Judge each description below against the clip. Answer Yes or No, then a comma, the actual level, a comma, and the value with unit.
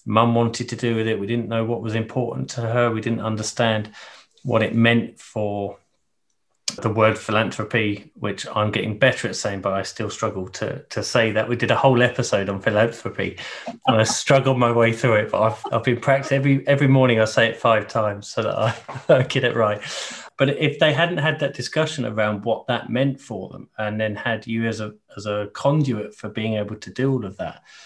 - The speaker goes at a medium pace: No, fast, 220 wpm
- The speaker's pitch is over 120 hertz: No, low, 115 Hz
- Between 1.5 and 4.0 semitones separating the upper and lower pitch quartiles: Yes, narrow, 2.5 semitones